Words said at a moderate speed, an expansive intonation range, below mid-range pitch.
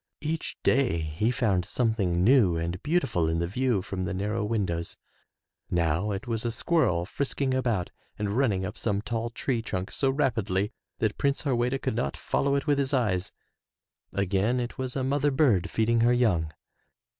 Yes: average, 175 wpm; wide, 5.9 semitones; low, 110 Hz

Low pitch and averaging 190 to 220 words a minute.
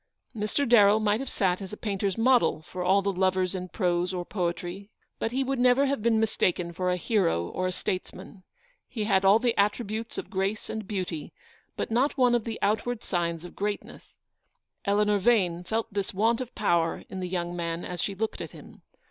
No: high, 200 Hz; fast, 205 wpm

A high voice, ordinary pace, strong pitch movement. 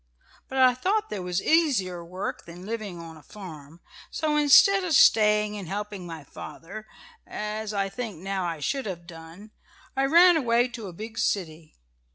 Yes: high, 210 Hz; average, 175 wpm; wide, 6.0 semitones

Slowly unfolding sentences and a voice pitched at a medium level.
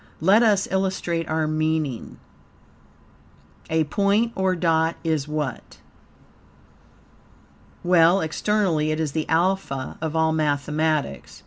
Yes: slow, 105 wpm; medium, 160 Hz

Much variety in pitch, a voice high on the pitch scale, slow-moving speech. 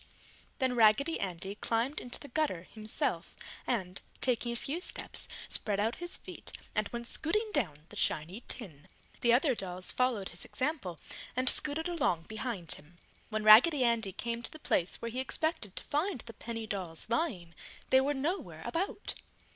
No: wide, 6.1 semitones; high, 235 Hz; average, 170 wpm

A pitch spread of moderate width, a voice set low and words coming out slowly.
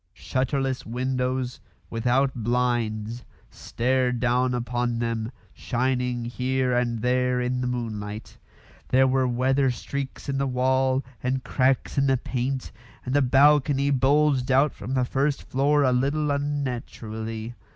No: narrow, 1.7 semitones; low, 125 Hz; slow, 130 wpm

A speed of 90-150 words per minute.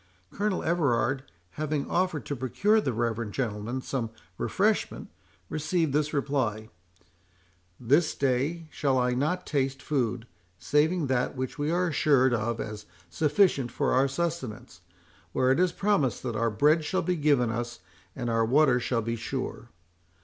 Yes: average, 145 wpm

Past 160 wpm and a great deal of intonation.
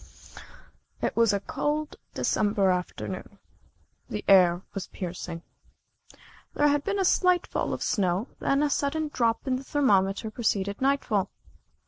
No: slow, 135 wpm; wide, 6.8 semitones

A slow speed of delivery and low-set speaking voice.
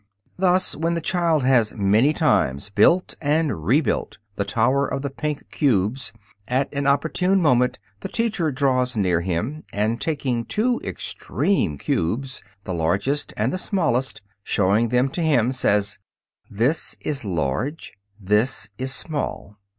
No: average, 145 wpm; low, 130 Hz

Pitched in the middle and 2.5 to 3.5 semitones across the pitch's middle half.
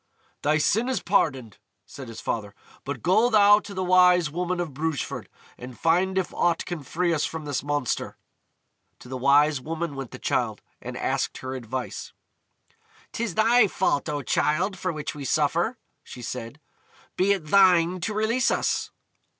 No: medium, 165 Hz; average, 5.1 semitones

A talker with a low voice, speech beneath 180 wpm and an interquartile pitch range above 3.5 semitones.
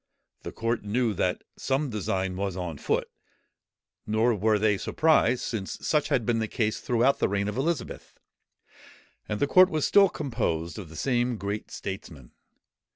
Yes: low, 110 Hz; average, 160 wpm; average, 4.3 semitones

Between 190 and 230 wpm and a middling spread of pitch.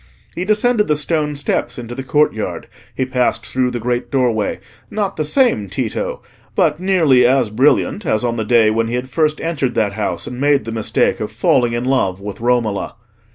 Yes: average, 195 wpm; average, 4.6 semitones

